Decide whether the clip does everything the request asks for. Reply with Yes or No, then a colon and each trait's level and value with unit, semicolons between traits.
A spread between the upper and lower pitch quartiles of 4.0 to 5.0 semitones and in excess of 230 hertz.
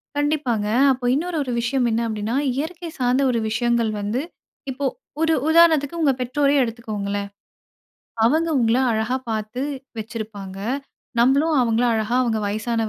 Yes: average, 4.4 semitones; high, 240 Hz